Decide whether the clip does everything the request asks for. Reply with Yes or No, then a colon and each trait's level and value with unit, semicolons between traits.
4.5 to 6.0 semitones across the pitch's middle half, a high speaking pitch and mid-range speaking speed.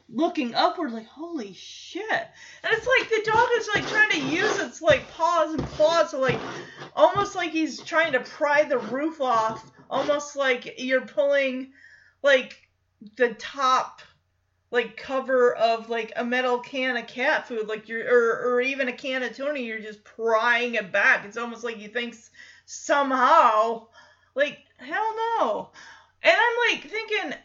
Yes: average, 5.2 semitones; very high, 270 Hz; average, 165 wpm